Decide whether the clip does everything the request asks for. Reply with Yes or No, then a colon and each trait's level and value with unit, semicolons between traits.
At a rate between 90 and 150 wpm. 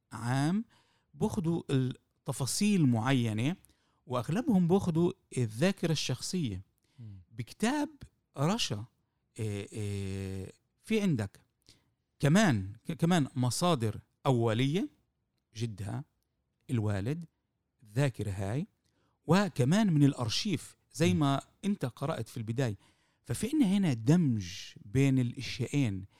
No: average, 80 wpm